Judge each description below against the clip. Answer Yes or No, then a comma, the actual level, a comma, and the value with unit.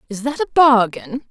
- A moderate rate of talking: Yes, average, 185 wpm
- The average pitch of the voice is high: Yes, very high, 250 Hz